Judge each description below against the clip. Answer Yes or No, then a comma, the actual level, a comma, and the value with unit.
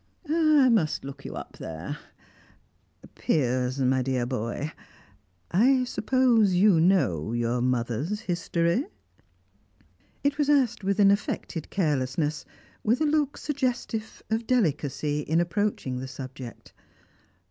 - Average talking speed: No, slow, 115 wpm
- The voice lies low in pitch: No, medium, 170 Hz